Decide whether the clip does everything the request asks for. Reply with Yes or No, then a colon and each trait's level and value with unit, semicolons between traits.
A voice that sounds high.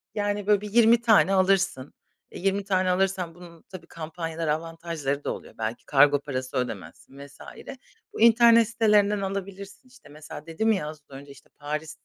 No: medium, 180 Hz